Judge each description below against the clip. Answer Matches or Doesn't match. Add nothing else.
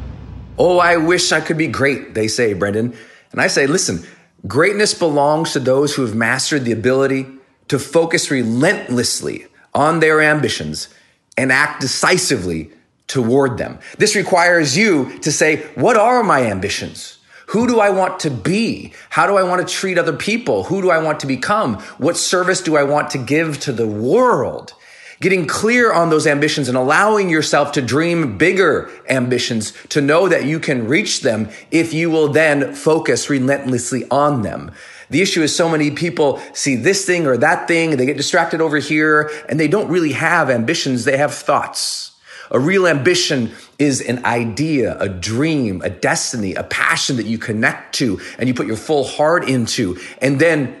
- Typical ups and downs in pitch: Matches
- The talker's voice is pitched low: Doesn't match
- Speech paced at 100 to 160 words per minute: Doesn't match